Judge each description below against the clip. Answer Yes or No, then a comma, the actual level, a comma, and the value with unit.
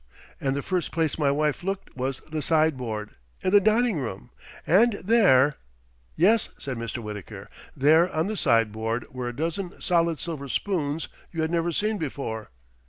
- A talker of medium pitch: Yes, medium, 155 Hz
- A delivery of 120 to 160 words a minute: No, average, 170 wpm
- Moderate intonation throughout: No, wide, 5.8 semitones